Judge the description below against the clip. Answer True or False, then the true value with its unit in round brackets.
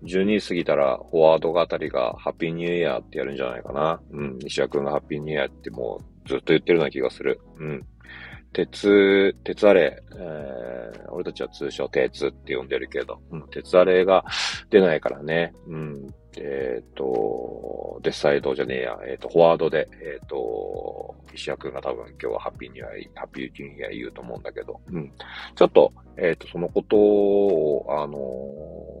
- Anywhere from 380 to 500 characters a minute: True (390 characters per minute)